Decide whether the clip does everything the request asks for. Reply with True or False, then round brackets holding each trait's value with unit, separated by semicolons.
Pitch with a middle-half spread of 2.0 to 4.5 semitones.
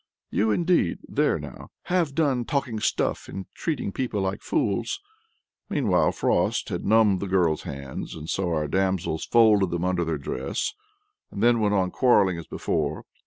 False (5.3 semitones)